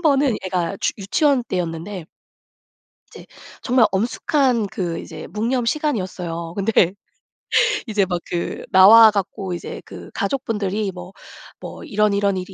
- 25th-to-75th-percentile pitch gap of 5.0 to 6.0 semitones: No, average, 4.1 semitones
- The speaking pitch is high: Yes, high, 200 Hz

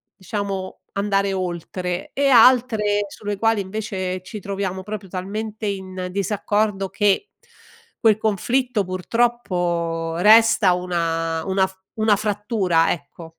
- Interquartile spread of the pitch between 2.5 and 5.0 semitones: Yes, average, 2.8 semitones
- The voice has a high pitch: Yes, high, 195 Hz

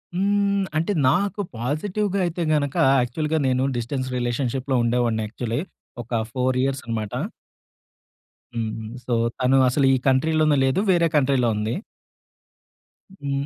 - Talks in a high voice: No, low, 135 Hz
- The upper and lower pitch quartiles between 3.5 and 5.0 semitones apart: Yes, average, 4.6 semitones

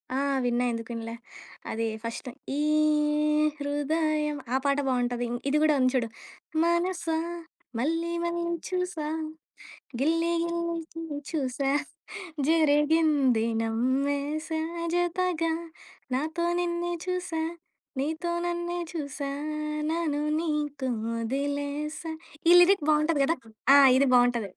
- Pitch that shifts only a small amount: No, average, 3.9 semitones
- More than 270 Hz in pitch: Yes, very high, 300 Hz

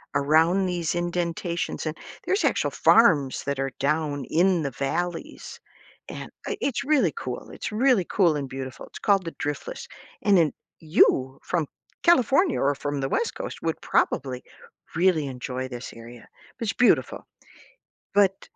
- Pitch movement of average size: No, wide, 5.8 semitones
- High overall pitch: No, medium, 165 Hz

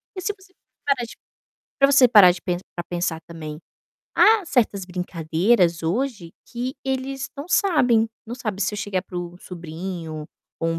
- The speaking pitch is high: Yes, high, 195 Hz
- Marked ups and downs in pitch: Yes, wide, 7.3 semitones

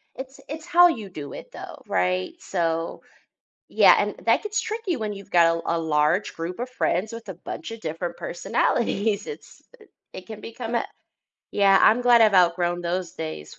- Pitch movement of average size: No, wide, 5.8 semitones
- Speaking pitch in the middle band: No, high, 195 Hz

